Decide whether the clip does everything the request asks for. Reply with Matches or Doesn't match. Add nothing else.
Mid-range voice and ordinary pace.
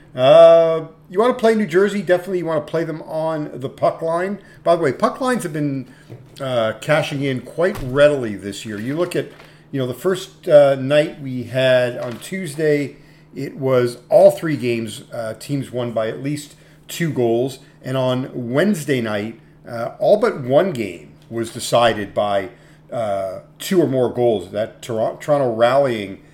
Matches